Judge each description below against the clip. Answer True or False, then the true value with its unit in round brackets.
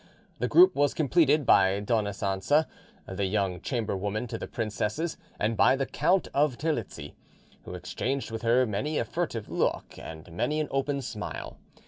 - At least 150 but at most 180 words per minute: True (160 wpm)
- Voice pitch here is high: False (115 Hz)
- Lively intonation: True (6.3 semitones)